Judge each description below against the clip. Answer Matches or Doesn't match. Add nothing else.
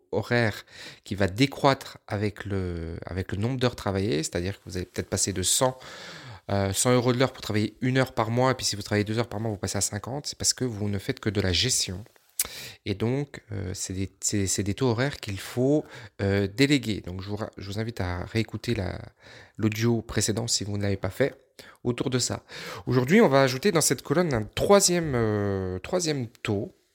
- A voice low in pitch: Matches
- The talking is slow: Doesn't match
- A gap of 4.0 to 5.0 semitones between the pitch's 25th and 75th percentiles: Matches